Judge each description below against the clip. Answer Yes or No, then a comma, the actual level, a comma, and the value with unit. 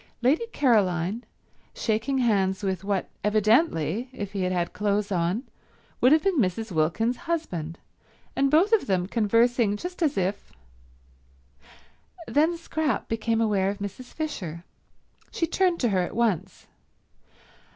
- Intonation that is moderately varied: No, wide, 6.1 semitones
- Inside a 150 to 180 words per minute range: No, slow, 135 wpm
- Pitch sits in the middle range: No, high, 215 Hz